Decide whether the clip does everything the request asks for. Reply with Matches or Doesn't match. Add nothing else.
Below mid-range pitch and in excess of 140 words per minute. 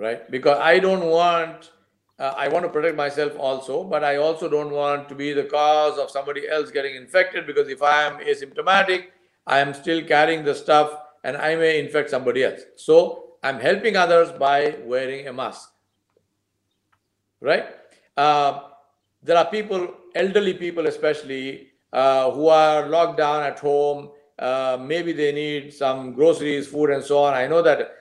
Doesn't match